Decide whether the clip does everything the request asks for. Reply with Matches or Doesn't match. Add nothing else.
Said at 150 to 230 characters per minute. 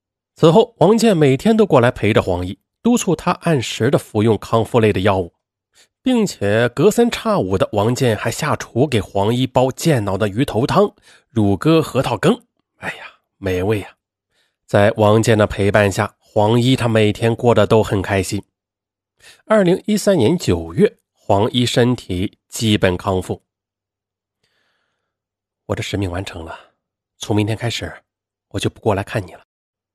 Matches